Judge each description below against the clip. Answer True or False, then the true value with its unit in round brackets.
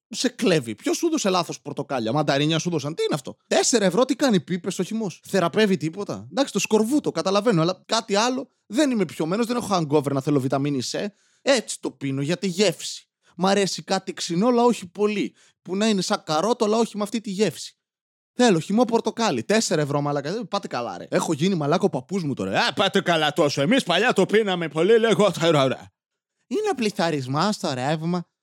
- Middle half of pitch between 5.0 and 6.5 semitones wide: True (5.6 semitones)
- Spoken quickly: True (200 wpm)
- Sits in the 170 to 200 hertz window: True (190 Hz)